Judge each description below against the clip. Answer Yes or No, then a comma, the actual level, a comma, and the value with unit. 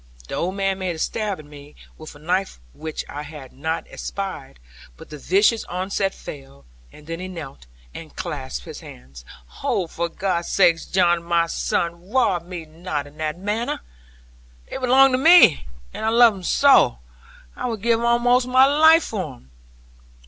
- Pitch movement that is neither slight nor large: No, wide, 6.2 semitones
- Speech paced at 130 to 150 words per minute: No, average, 175 wpm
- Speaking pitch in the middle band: Yes, medium, 180 Hz